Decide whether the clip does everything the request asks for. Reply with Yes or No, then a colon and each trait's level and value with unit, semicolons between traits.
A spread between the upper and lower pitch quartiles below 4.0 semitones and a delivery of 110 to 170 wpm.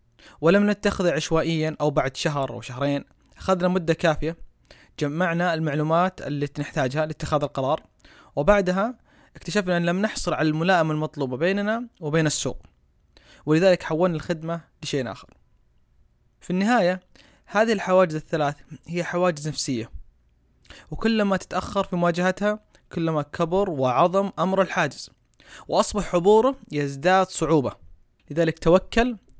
No: average, 4.4 semitones; average, 115 wpm